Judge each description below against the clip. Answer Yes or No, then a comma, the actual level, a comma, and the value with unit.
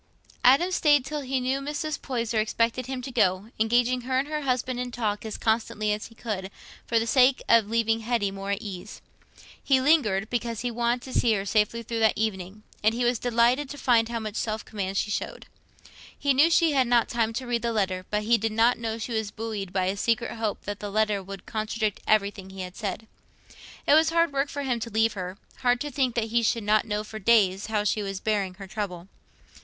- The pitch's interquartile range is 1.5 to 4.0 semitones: Yes, average, 3.1 semitones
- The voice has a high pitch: Yes, high, 225 Hz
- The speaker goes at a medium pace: No, fast, 230 wpm